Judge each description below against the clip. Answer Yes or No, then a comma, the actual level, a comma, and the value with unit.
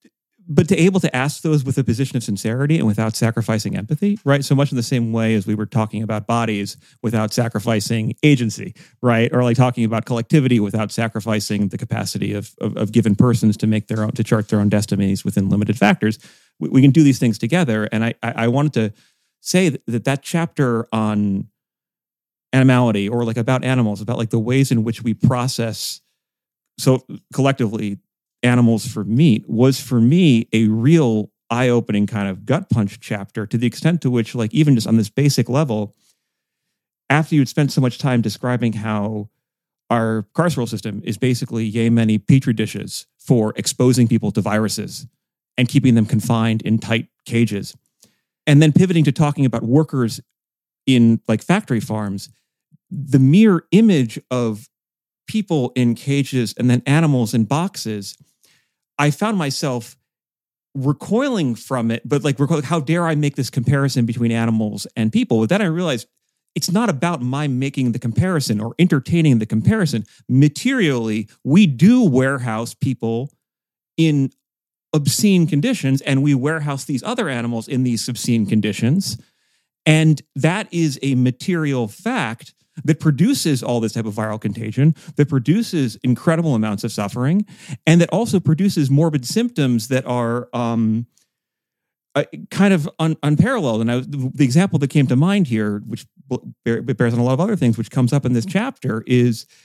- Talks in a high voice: No, low, 125 Hz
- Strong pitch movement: No, average, 4.7 semitones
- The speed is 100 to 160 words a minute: No, average, 170 wpm